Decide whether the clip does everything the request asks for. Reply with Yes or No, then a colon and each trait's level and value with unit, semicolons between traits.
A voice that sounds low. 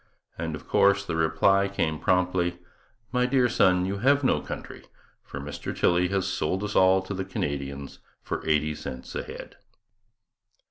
Yes: very low, 90 Hz